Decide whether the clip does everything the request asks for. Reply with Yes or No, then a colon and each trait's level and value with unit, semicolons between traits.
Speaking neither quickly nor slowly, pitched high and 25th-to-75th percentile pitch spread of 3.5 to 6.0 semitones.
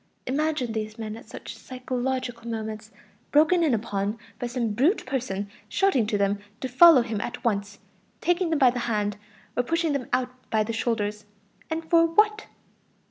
Yes: average, 170 wpm; high, 245 Hz; average, 5.2 semitones